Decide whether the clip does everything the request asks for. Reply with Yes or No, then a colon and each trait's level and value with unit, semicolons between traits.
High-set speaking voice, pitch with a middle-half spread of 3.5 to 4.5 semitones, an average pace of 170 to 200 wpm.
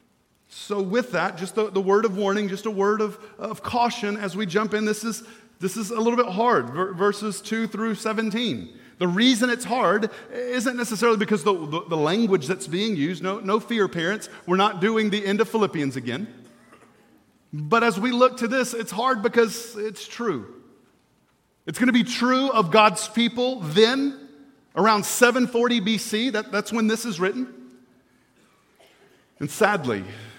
No: high, 215 Hz; average, 2.9 semitones; average, 175 wpm